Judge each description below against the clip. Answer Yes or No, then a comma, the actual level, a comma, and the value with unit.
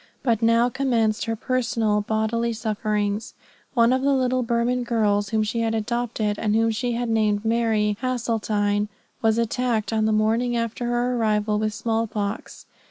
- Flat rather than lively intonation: Yes, narrow, 1.9 semitones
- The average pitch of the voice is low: No, high, 225 Hz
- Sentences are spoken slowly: No, average, 165 wpm